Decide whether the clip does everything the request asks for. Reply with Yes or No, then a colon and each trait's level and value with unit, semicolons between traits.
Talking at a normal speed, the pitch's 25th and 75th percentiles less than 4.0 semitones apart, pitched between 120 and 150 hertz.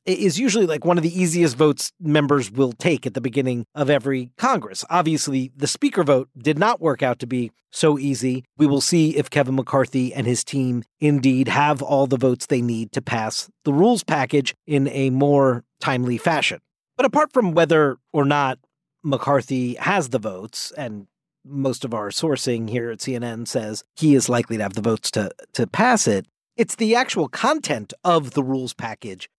Yes: average, 190 wpm; average, 3.6 semitones; medium, 140 Hz